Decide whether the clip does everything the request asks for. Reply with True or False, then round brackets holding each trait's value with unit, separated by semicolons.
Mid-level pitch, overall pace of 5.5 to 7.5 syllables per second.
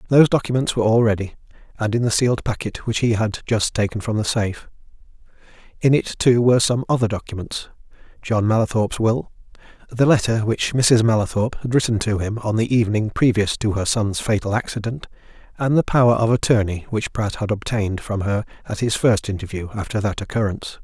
False (110 Hz; 6.0 syllables/s)